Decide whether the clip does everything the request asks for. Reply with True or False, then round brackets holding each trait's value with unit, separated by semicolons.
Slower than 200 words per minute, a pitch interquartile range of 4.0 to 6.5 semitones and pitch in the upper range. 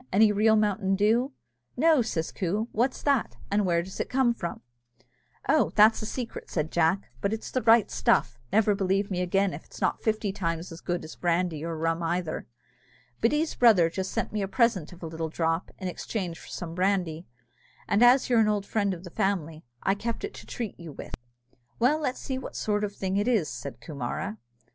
False (205 wpm; 4.6 semitones; 195 Hz)